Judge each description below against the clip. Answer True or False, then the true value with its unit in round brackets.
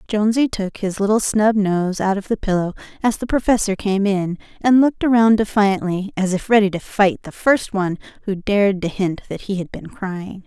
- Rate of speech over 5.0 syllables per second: True (5.2 syllables/s)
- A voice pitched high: True (200 Hz)